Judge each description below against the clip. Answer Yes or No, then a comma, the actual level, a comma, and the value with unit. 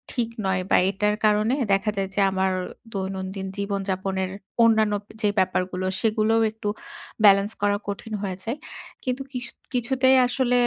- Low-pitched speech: No, high, 205 Hz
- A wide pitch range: No, average, 2.9 semitones